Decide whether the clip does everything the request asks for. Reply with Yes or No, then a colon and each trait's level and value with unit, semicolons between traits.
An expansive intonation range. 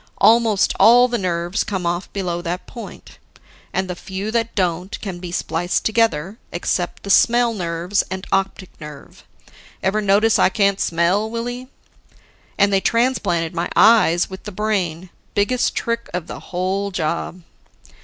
No: average, 3.9 semitones